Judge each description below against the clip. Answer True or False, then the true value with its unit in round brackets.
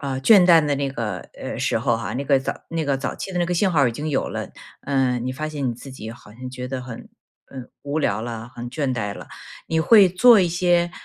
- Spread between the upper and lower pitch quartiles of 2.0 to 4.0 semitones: False (5.0 semitones)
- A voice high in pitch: False (135 Hz)